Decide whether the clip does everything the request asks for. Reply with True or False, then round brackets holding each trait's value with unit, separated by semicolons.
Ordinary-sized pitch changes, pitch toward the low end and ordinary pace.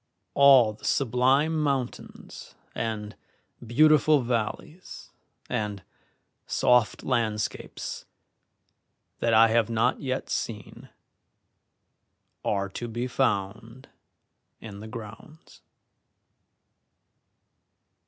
False (3.6 semitones; 120 Hz; 75 wpm)